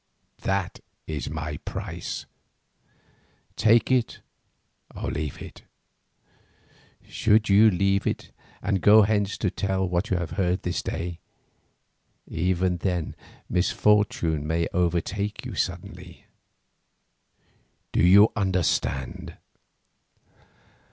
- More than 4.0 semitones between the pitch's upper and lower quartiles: No, average, 3.2 semitones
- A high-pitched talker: No, very low, 95 Hz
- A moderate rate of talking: No, slow, 100 wpm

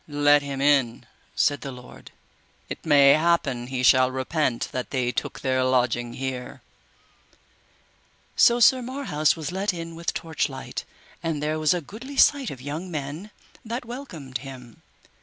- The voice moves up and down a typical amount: Yes, average, 4.6 semitones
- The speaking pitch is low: No, medium, 145 Hz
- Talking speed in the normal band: Yes, average, 150 wpm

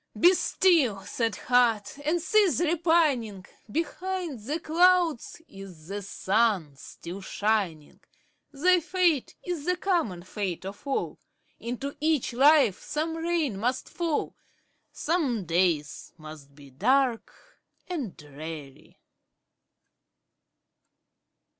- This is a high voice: Yes, high, 245 Hz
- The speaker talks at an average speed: No, slow, 105 wpm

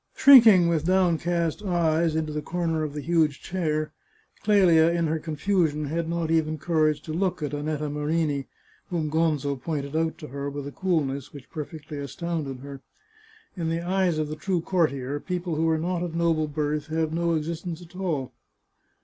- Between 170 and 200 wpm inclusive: Yes, average, 180 wpm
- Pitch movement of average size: No, narrow, 2.3 semitones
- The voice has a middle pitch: Yes, medium, 160 Hz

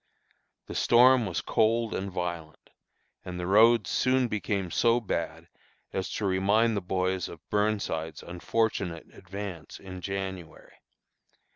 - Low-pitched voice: Yes, very low, 95 Hz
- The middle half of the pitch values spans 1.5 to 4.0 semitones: Yes, average, 3.6 semitones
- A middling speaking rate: No, slow, 125 wpm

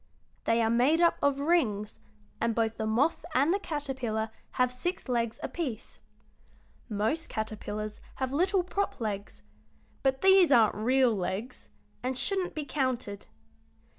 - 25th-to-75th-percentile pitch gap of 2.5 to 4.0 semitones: No, wide, 5.5 semitones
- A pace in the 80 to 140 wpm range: Yes, slow, 135 wpm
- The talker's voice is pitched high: Yes, very high, 255 Hz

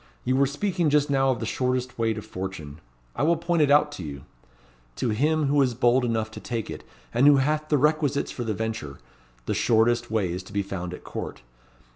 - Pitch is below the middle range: Yes, low, 125 Hz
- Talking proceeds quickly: Yes, fast, 220 wpm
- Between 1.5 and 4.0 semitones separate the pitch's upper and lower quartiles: No, average, 4.9 semitones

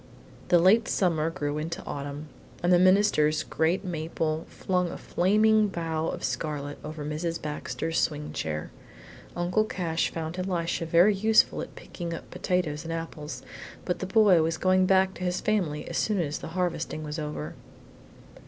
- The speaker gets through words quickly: No, average, 160 wpm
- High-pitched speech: No, medium, 165 Hz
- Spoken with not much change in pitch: No, average, 3.2 semitones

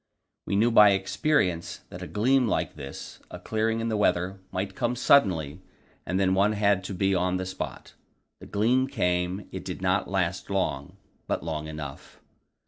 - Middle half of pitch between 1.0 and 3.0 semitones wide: No, average, 3.4 semitones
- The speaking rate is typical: Yes, average, 175 wpm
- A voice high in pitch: No, very low, 95 Hz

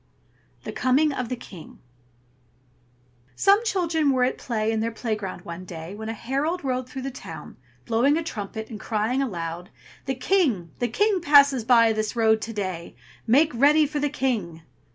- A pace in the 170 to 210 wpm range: Yes, average, 175 wpm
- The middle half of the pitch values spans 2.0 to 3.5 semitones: No, average, 4.8 semitones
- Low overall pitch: No, high, 245 Hz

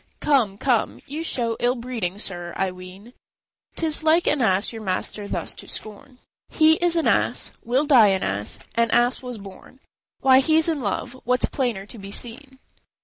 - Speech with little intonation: No, average, 5.3 semitones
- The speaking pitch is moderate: No, high, 240 Hz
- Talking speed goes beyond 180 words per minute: Yes, average, 190 wpm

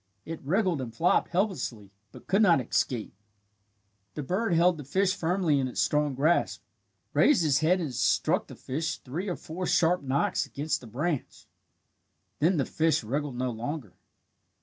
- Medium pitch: Yes, medium, 155 Hz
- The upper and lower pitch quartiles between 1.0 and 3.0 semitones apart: No, average, 4.9 semitones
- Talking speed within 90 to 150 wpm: No, average, 165 wpm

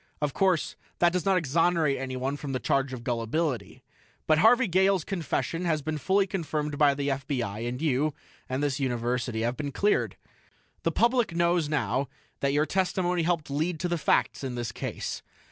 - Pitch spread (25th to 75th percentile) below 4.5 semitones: No, average, 4.8 semitones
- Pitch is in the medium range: Yes, medium, 150 Hz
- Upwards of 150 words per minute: Yes, average, 180 wpm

